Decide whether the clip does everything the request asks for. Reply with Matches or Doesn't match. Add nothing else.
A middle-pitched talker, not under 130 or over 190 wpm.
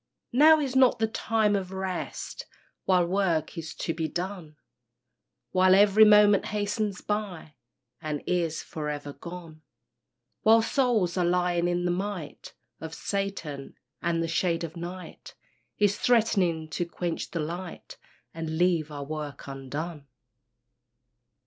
Matches